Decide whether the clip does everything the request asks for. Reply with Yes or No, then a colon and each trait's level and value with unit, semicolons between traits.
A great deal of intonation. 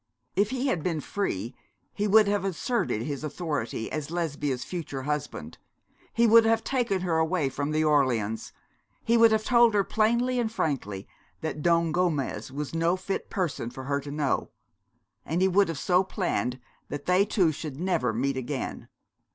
Yes: wide, 6.1 semitones